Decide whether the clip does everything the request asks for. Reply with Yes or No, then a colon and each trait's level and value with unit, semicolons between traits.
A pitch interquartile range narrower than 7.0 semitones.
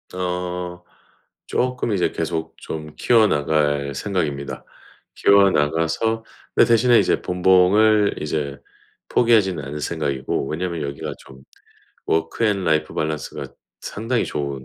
Yes: average, 5.1 semitones